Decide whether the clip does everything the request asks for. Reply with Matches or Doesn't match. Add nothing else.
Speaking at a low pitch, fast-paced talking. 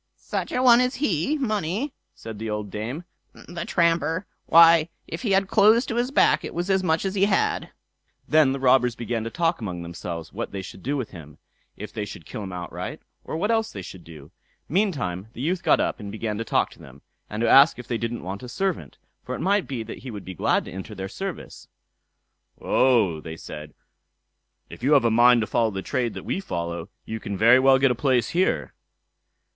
Matches